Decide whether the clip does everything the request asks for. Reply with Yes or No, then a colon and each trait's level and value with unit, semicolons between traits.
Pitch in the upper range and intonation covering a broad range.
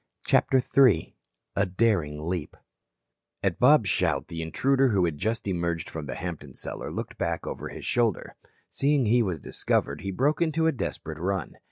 No: very low, 95 Hz; wide, 7.4 semitones